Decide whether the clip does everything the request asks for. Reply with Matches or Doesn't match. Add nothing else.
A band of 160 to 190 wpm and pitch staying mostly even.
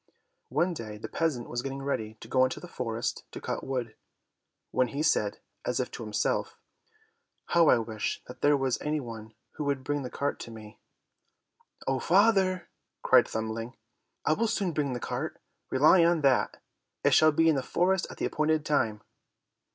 Doesn't match